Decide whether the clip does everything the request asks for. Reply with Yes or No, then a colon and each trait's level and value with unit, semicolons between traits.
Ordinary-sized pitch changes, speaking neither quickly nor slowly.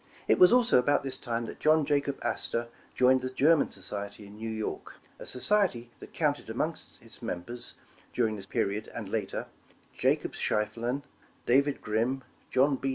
Yes: average, 4.1 semitones; average, 165 wpm